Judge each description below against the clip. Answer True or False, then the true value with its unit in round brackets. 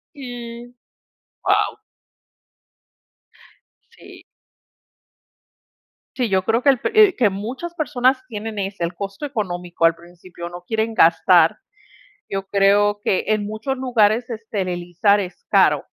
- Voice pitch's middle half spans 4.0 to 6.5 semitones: True (4.6 semitones)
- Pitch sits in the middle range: False (205 Hz)